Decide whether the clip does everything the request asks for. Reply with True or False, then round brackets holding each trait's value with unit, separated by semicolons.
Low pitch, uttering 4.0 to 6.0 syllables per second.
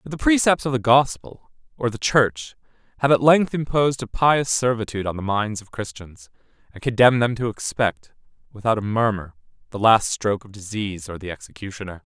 True (115 Hz; 5.5 syllables/s)